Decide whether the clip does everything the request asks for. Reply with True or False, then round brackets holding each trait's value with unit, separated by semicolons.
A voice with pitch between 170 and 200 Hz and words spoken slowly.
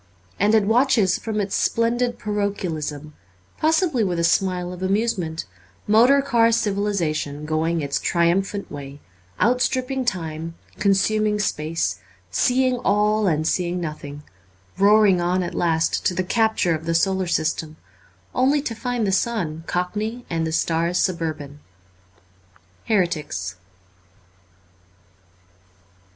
True (185 Hz; 120 wpm)